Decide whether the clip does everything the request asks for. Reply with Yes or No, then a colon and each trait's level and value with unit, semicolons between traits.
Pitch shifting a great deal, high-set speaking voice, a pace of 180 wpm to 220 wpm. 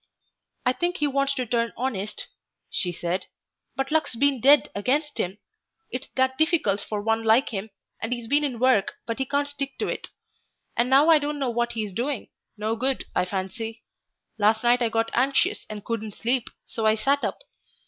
No: average, 4.0 semitones; high, 240 Hz; average, 190 wpm